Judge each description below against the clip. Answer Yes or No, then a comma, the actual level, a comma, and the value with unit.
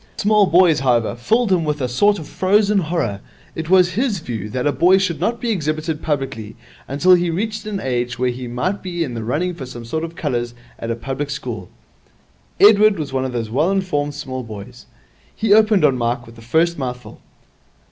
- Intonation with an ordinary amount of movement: No, wide, 7.1 semitones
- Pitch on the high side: No, medium, 150 Hz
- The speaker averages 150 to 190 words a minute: No, fast, 205 wpm